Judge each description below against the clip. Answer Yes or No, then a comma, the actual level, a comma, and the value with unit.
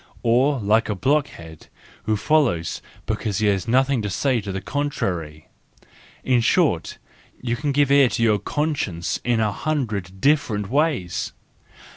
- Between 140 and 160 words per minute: Yes, average, 145 wpm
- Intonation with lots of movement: Yes, wide, 6.2 semitones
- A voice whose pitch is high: No, low, 115 Hz